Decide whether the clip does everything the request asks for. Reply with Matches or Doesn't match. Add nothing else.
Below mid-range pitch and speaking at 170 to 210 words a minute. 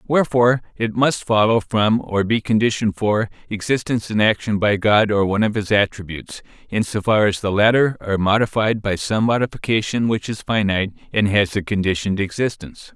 Matches